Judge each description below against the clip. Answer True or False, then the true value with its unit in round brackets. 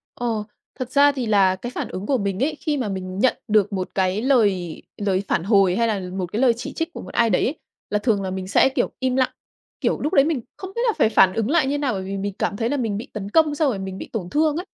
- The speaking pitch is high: True (220 Hz)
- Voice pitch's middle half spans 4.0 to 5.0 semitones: False (5.6 semitones)